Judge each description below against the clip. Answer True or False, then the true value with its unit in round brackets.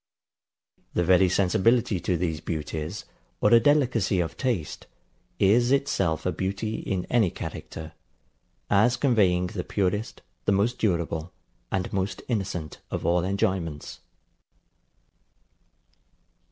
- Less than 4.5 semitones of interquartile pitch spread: True (4.0 semitones)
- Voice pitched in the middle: False (95 Hz)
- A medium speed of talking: False (115 wpm)